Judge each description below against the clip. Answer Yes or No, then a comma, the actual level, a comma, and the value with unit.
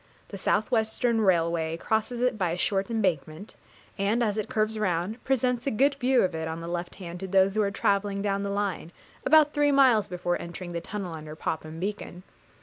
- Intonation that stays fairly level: No, average, 4.2 semitones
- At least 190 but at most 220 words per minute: Yes, fast, 205 wpm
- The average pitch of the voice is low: No, high, 200 Hz